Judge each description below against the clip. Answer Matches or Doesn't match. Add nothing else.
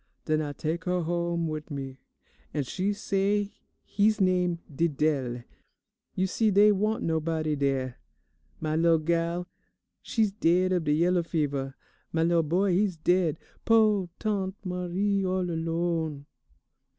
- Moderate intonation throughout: Matches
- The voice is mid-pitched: Matches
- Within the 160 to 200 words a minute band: Doesn't match